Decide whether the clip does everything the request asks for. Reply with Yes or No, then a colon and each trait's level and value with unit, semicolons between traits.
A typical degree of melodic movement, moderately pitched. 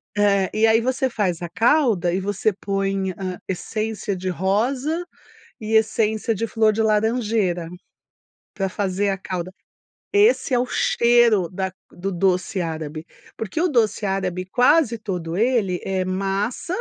No: average, 3.4 semitones; high, 205 Hz